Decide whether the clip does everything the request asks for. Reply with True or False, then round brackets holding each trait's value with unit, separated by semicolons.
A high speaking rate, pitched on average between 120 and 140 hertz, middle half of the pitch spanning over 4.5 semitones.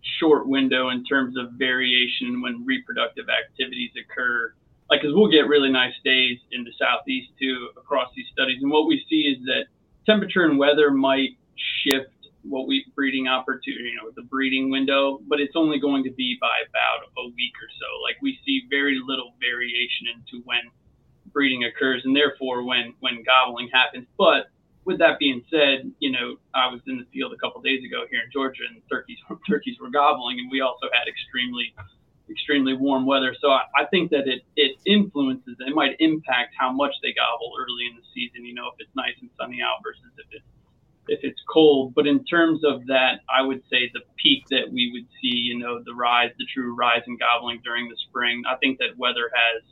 False (210 wpm; 135 Hz; 3.6 semitones)